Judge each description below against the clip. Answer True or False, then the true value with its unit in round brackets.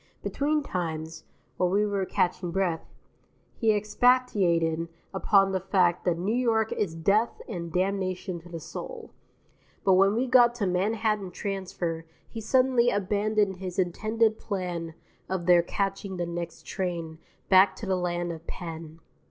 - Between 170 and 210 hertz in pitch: True (190 Hz)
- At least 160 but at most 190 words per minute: False (145 wpm)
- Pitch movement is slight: False (3.6 semitones)